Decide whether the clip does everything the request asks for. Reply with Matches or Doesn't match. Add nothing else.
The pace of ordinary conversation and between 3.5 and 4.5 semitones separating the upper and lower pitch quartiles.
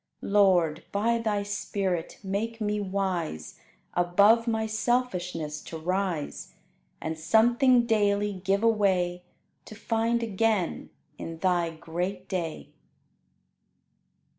Doesn't match